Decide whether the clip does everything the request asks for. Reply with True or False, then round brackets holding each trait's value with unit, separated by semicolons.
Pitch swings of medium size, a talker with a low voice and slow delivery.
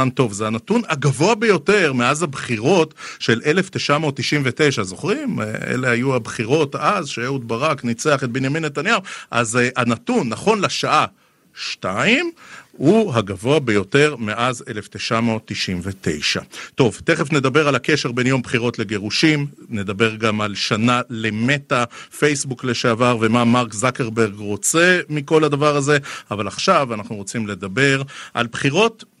False (4.7 semitones; 130 Hz; 125 wpm)